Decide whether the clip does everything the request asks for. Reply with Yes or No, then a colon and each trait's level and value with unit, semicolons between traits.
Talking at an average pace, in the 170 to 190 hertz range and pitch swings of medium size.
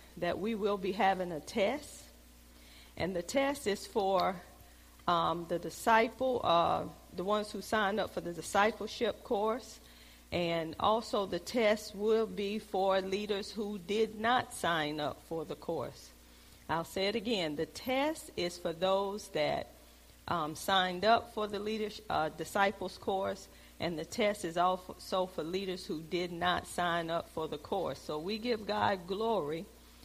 Yes: average, 160 wpm; medium, 185 Hz; average, 4.7 semitones